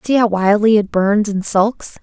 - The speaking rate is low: No, fast, 205 wpm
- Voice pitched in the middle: No, high, 210 Hz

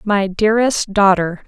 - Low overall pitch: No, high, 200 Hz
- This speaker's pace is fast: No, slow, 120 wpm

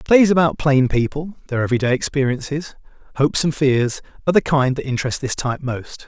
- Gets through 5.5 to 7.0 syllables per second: Yes, 6.0 syllables/s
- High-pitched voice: No, medium, 140 Hz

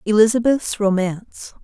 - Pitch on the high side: Yes, high, 215 Hz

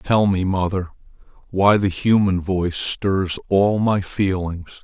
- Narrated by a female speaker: No, male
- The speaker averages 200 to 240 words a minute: No, slow, 135 wpm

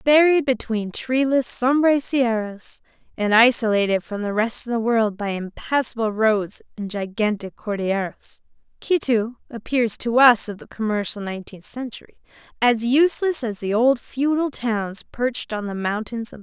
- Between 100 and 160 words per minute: Yes, average, 155 wpm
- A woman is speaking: Yes, female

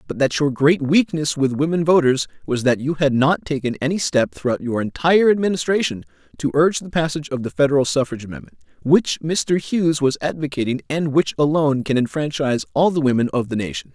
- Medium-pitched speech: Yes, medium, 145 Hz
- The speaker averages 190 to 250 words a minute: Yes, average, 195 wpm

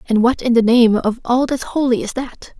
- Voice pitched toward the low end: No, high, 240 Hz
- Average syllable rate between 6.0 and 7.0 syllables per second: No, 4.9 syllables/s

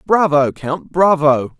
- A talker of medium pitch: Yes, medium, 155 Hz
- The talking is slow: Yes, slow, 115 wpm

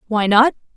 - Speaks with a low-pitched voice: No, high, 230 Hz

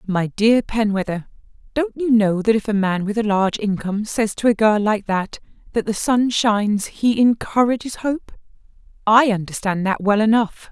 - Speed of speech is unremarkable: Yes, average, 180 wpm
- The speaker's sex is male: No, female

